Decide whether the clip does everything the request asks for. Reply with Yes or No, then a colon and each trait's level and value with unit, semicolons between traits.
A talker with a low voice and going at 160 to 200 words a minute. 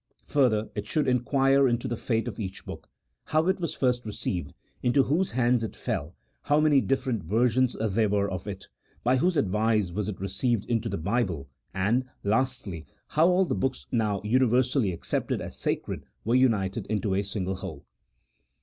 Yes: low, 115 Hz; average, 175 wpm